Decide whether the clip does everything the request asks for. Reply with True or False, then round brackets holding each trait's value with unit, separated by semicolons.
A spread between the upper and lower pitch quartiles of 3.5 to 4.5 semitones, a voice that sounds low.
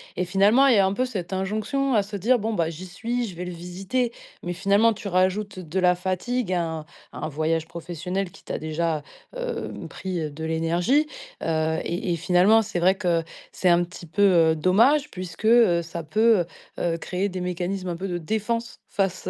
False (3.8 semitones; 185 Hz)